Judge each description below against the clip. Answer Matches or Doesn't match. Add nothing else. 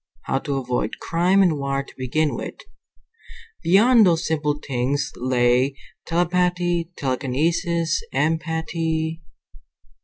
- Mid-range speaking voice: Matches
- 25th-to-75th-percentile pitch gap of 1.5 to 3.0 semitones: Doesn't match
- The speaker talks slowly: Matches